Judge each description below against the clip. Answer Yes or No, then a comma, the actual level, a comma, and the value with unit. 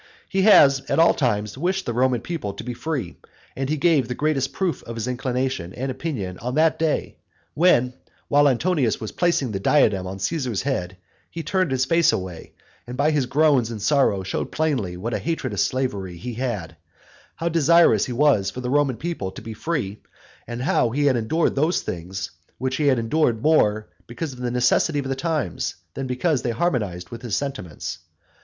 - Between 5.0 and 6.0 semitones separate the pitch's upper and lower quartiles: Yes, wide, 5.4 semitones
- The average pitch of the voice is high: No, low, 130 Hz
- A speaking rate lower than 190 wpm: No, average, 195 wpm